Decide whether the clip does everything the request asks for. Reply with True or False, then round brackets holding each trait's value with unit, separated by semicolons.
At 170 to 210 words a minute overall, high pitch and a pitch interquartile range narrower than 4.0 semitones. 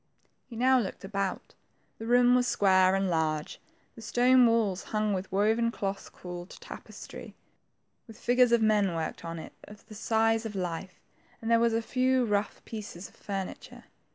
True (175 wpm; 215 Hz; 3.5 semitones)